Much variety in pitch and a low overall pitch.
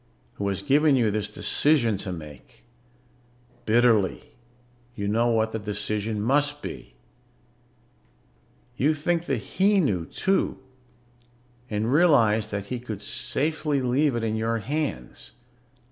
Yes: wide, 5.7 semitones; low, 115 Hz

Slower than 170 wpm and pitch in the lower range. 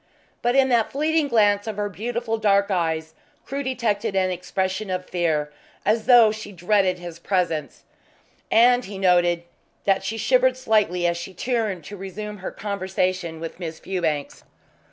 No: average, 155 wpm; high, 195 Hz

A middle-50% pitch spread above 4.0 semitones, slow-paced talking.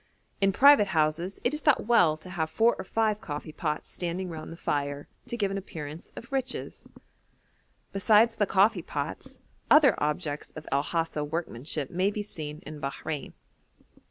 No: wide, 5.4 semitones; average, 165 wpm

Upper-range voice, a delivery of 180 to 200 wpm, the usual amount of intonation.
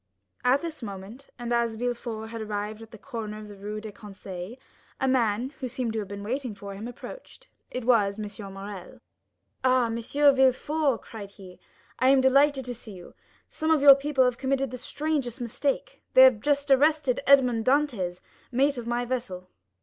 Yes: high, 240 Hz; average, 185 wpm; average, 4.2 semitones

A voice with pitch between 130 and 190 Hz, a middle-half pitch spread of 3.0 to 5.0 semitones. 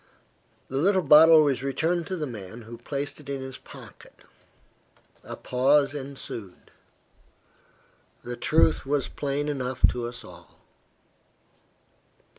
Yes: medium, 140 Hz; average, 3.3 semitones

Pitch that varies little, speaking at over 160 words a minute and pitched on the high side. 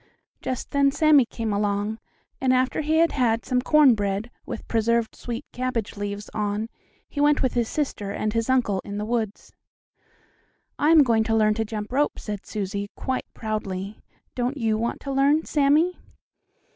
No: average, 4.5 semitones; average, 170 wpm; high, 230 Hz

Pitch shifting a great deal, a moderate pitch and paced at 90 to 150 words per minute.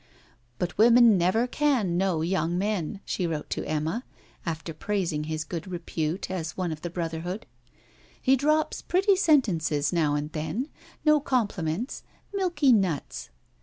Yes: wide, 7.0 semitones; medium, 180 Hz; average, 140 wpm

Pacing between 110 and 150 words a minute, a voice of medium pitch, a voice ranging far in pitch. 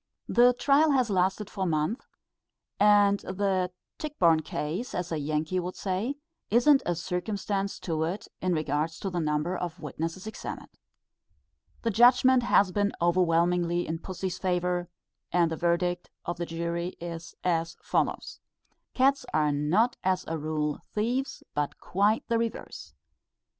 No: average, 140 wpm; medium, 180 Hz; average, 3.9 semitones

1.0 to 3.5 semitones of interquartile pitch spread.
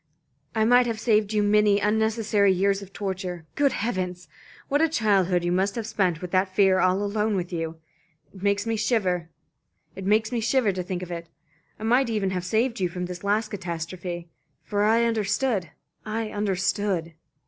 Yes: average, 3.2 semitones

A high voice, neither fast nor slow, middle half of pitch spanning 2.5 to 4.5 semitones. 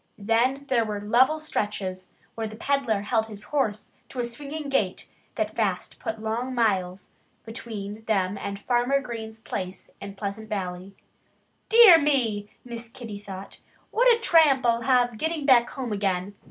Yes: high, 225 Hz; average, 155 wpm; average, 4.2 semitones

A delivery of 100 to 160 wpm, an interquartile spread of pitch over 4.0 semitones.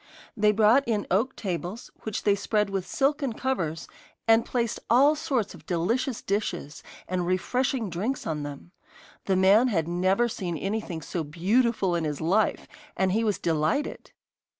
Yes: average, 155 wpm; average, 5.0 semitones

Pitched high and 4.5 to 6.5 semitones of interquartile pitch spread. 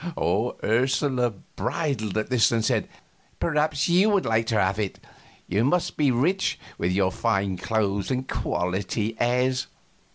No: low, 115 Hz; average, 5.1 semitones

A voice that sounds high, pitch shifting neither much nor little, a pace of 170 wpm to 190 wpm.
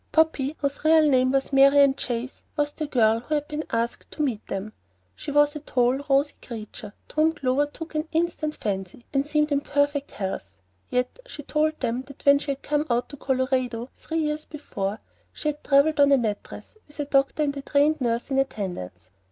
No: very high, 280 Hz; average, 3.6 semitones; average, 200 wpm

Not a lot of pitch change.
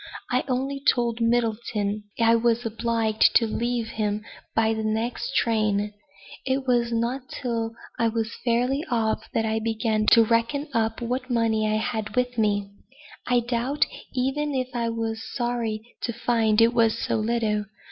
Yes: narrow, 1.7 semitones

